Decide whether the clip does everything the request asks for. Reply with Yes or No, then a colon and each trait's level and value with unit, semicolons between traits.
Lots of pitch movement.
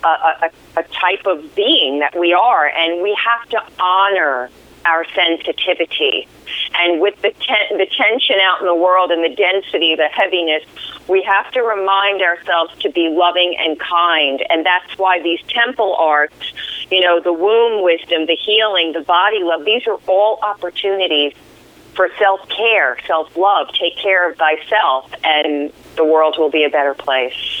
No: average, 3.6 semitones